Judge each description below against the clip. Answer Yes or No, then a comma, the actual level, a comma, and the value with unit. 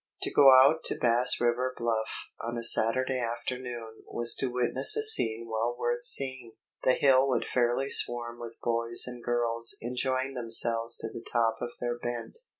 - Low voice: Yes, low, 120 Hz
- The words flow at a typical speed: Yes, average, 170 wpm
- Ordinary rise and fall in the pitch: No, narrow, 1.8 semitones